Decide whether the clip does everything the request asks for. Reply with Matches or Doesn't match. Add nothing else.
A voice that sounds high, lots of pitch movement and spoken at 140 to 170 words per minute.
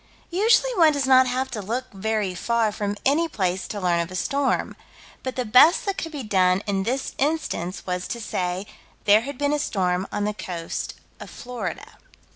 Doesn't match